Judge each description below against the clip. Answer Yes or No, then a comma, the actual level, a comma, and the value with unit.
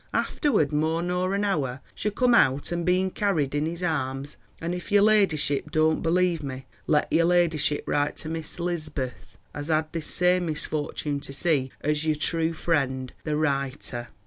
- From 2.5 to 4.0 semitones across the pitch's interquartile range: Yes, average, 3.4 semitones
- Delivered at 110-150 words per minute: No, average, 170 wpm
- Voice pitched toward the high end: No, medium, 155 Hz